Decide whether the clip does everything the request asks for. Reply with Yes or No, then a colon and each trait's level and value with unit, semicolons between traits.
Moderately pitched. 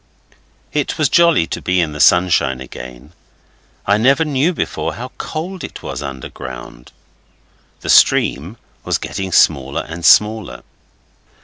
No: very low, 90 Hz